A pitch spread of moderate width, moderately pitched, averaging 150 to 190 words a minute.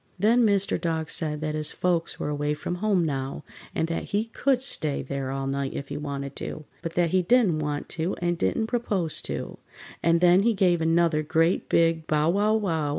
No: average, 3.9 semitones; medium, 165 Hz; fast, 205 wpm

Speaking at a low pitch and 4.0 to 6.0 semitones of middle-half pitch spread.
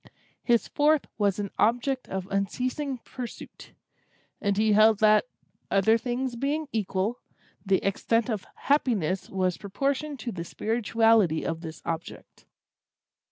No: high, 220 Hz; average, 4.4 semitones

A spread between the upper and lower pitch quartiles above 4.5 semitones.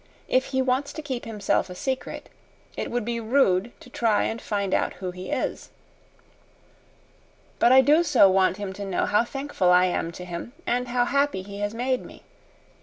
Yes: average, 5.2 semitones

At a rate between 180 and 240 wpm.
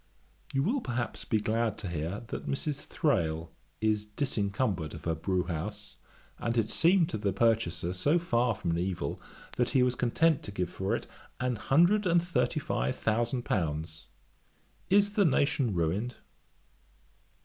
No: average, 160 wpm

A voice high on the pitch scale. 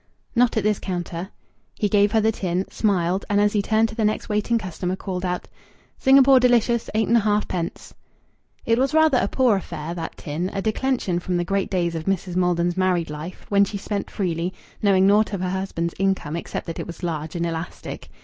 Yes: high, 195 Hz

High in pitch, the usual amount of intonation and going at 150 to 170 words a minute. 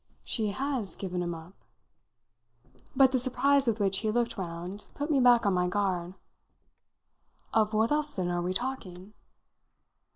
No: high, 210 Hz; wide, 5.7 semitones; average, 155 wpm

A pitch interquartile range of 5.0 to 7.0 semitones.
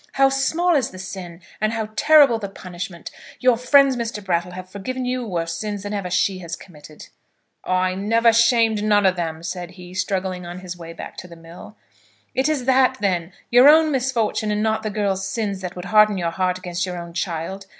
No: average, 4.3 semitones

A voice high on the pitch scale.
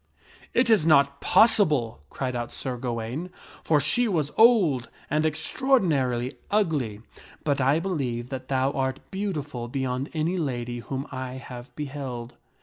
No: low, 135 Hz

